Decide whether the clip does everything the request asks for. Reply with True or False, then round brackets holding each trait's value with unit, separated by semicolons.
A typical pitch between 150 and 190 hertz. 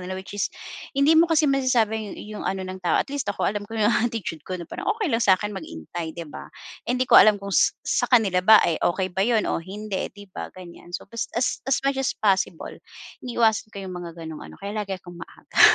False (205 Hz)